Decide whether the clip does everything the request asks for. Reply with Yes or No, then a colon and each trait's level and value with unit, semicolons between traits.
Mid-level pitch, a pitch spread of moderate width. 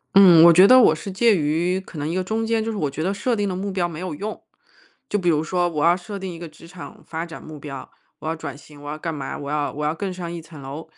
Yes: medium, 170 Hz; average, 3.7 semitones